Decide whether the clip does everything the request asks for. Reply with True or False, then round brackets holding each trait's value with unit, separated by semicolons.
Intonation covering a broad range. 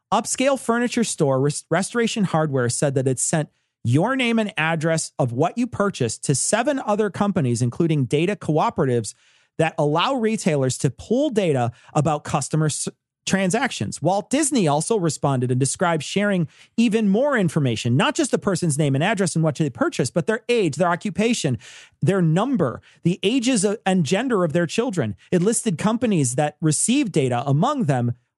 True (6.6 semitones)